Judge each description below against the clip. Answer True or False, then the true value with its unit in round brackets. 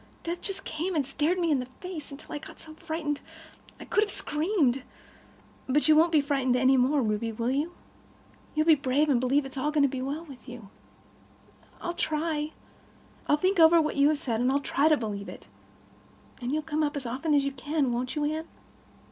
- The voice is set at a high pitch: True (295 Hz)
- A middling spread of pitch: True (3.3 semitones)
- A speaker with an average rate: False (215 wpm)